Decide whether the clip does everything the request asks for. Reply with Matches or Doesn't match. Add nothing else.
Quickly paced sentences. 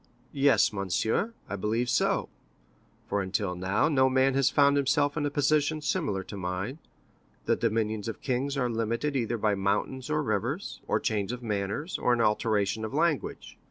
Doesn't match